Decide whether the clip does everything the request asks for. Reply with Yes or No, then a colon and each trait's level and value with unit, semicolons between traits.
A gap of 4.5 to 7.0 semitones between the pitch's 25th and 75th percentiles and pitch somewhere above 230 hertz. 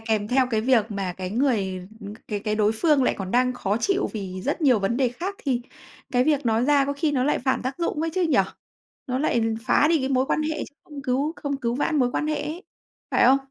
Yes: average, 4.9 semitones; very high, 255 Hz